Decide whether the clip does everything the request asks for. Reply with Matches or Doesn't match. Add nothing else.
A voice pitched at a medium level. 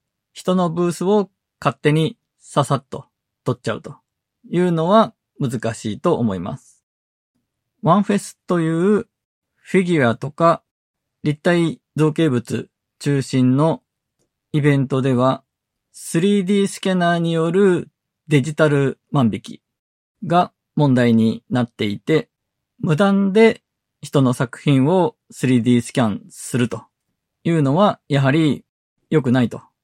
Matches